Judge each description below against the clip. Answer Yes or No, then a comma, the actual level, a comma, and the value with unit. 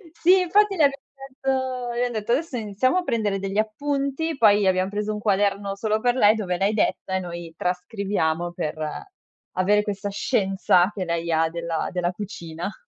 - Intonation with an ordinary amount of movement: Yes, average, 5.0 semitones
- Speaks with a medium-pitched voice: No, high, 205 Hz